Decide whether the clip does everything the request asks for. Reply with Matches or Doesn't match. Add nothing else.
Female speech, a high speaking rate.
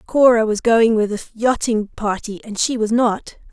Doesn't match